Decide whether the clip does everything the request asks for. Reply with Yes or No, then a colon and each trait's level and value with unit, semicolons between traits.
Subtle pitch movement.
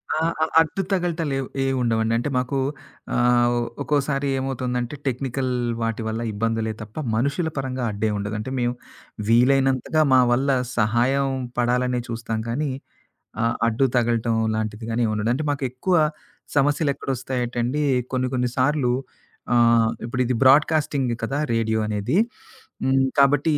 No: average, 3.1 semitones